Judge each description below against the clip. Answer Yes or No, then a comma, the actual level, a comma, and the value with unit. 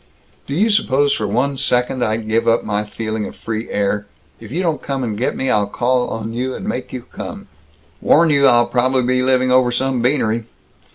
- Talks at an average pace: No, fast, 210 wpm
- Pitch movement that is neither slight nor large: Yes, average, 3.0 semitones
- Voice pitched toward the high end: No, low, 125 Hz